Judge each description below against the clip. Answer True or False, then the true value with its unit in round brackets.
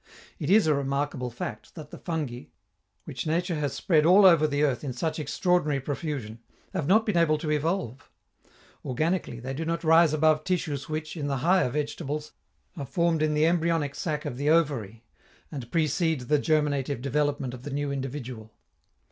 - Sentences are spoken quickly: False (175 wpm)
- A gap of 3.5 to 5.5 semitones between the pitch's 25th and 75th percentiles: False (3.0 semitones)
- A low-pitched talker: False (150 Hz)